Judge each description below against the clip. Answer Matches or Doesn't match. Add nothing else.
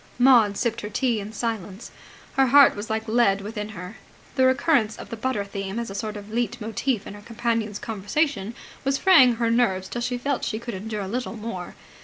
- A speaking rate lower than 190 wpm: Doesn't match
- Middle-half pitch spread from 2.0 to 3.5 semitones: Matches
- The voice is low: Doesn't match